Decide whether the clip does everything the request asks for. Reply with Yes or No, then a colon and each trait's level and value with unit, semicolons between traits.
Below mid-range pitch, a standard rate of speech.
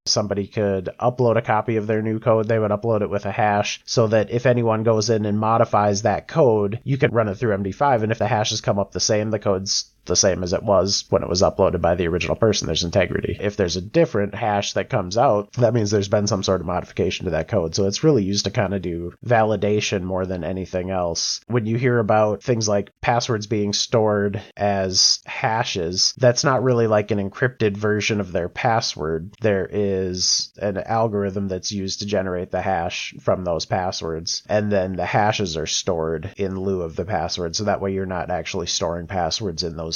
No: low, 105 Hz; fast, 220 wpm